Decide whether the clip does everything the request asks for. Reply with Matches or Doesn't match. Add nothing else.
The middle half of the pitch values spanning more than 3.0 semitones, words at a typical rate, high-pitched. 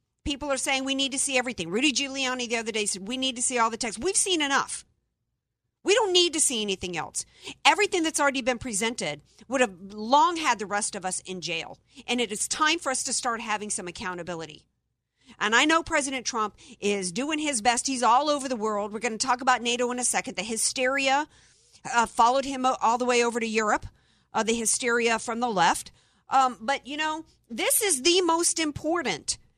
Doesn't match